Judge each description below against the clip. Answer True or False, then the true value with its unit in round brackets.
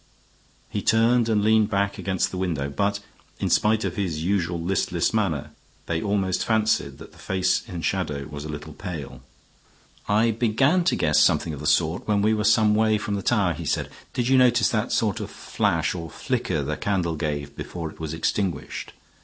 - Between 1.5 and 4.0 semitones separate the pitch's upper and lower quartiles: False (4.8 semitones)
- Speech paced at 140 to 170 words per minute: False (195 wpm)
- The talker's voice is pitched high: False (95 Hz)